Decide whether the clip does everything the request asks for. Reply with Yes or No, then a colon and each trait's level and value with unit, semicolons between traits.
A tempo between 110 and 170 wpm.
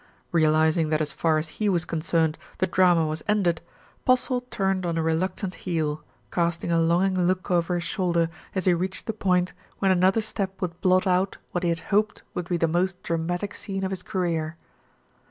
No: average, 190 wpm